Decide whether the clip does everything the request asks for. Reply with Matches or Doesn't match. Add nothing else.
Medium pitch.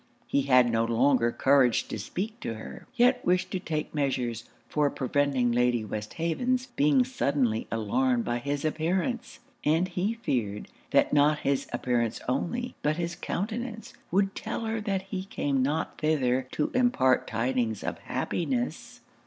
Matches